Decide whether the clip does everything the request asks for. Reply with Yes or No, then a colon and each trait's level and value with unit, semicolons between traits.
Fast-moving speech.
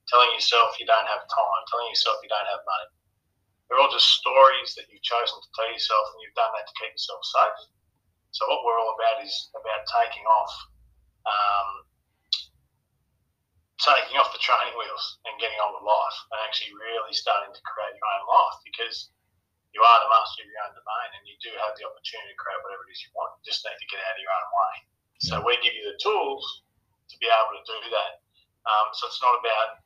Yes: fast, 215 wpm